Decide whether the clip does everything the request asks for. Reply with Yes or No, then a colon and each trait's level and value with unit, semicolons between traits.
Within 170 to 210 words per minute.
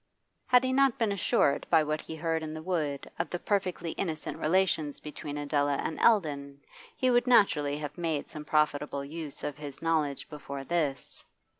Yes: average, 175 wpm